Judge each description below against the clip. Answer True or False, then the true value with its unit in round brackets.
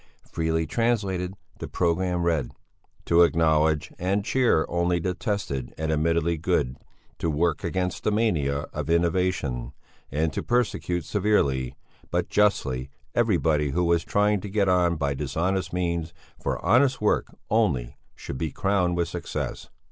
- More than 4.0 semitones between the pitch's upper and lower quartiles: False (3.7 semitones)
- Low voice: True (85 Hz)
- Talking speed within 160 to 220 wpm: False (140 wpm)